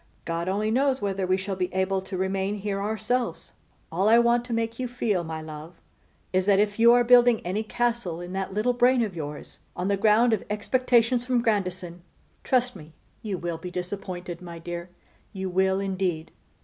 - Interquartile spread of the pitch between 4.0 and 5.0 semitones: Yes, average, 4.3 semitones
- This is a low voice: No, high, 195 Hz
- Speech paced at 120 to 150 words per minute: No, average, 190 wpm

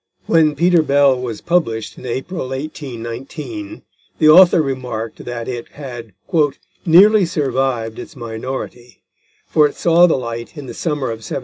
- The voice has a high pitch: No, low, 135 Hz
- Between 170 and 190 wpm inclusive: No, average, 145 wpm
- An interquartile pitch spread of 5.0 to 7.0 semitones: Yes, average, 5.3 semitones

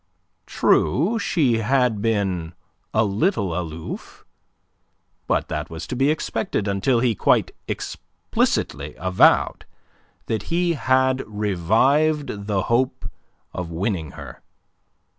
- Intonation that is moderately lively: No, wide, 5.9 semitones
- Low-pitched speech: Yes, low, 110 Hz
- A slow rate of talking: Yes, slow, 105 wpm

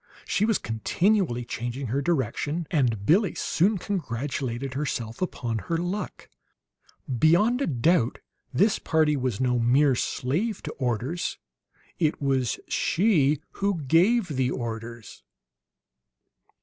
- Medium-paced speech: No, slow, 115 wpm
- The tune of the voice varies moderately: No, wide, 6.4 semitones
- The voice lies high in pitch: No, medium, 140 Hz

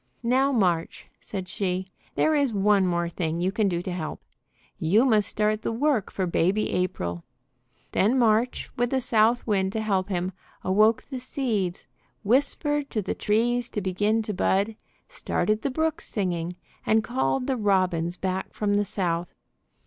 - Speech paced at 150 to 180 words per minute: Yes, average, 165 wpm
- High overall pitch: Yes, high, 210 Hz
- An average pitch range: Yes, average, 4.5 semitones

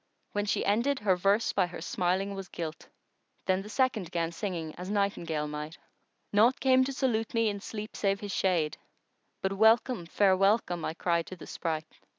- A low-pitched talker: No, high, 195 Hz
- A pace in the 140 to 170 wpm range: No, average, 190 wpm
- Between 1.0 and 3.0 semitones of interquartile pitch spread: No, average, 3.8 semitones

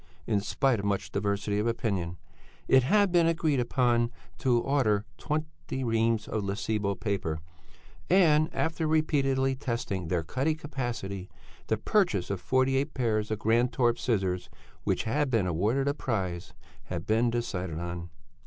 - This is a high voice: No, low, 115 Hz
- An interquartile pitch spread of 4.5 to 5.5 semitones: Yes, average, 5.1 semitones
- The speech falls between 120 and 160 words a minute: Yes, average, 145 wpm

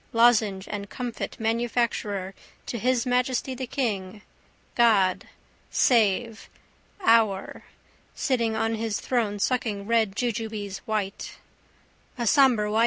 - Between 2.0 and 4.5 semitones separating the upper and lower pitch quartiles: Yes, average, 2.8 semitones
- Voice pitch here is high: Yes, high, 225 Hz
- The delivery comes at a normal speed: No, slow, 105 wpm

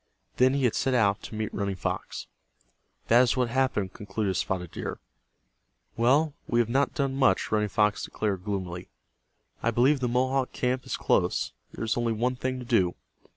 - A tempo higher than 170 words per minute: Yes, average, 180 wpm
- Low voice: Yes, low, 120 Hz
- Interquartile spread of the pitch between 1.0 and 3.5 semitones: No, average, 3.9 semitones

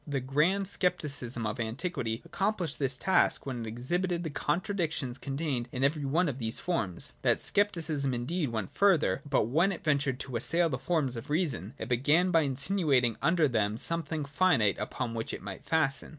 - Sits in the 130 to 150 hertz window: Yes, medium, 140 Hz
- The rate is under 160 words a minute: No, average, 180 wpm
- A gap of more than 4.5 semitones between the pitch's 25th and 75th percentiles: Yes, wide, 5.5 semitones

